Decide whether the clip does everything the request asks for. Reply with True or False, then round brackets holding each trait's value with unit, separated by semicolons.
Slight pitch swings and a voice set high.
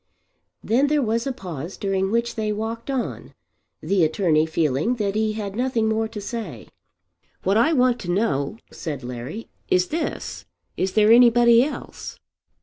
False (4.6 semitones; 215 Hz)